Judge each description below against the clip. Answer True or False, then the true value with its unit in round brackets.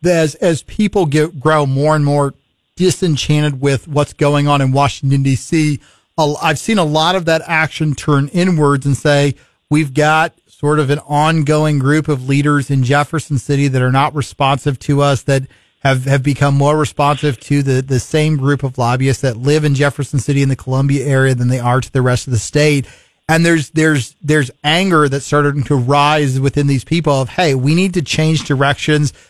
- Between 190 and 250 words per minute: True (195 wpm)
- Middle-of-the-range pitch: True (145 Hz)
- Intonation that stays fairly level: True (1.8 semitones)